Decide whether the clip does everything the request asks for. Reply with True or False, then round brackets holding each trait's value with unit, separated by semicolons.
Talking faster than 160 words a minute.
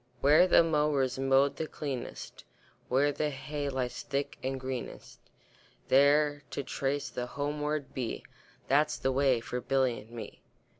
False (145 wpm)